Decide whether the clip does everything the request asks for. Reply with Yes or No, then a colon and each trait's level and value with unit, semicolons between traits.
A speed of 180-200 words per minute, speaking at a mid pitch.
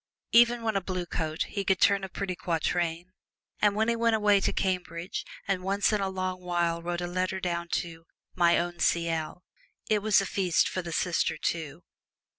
Yes: average, 195 wpm; medium, 180 Hz